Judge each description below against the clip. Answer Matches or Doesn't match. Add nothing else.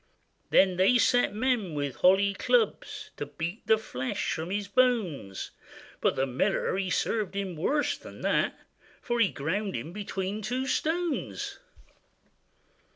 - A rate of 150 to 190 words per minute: Doesn't match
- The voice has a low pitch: Doesn't match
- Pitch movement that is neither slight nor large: Doesn't match